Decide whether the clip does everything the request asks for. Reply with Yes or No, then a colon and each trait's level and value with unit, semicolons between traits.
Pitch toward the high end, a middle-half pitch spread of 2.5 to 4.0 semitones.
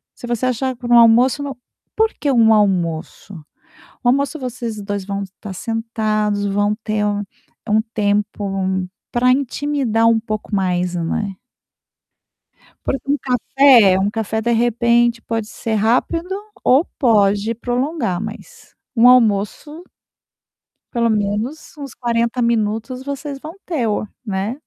Yes: high, 230 Hz; average, 3.5 semitones